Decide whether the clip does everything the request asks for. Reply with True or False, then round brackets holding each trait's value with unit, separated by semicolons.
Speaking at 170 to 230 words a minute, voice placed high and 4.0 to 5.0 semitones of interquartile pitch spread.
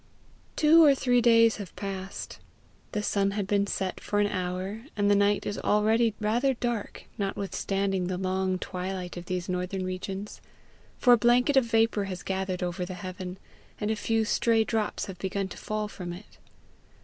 False (175 wpm; 200 Hz; 3.0 semitones)